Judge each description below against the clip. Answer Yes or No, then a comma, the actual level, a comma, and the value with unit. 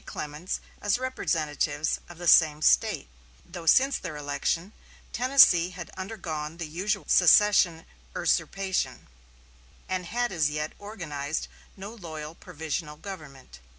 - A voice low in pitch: No, medium, 170 Hz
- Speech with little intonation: No, average, 4.4 semitones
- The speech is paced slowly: Yes, slow, 120 wpm